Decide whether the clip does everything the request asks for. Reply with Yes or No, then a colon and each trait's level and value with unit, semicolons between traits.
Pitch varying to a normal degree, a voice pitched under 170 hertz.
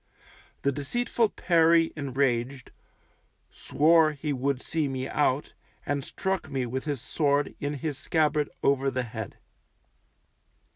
Yes: average, 3.0 semitones; medium, 140 Hz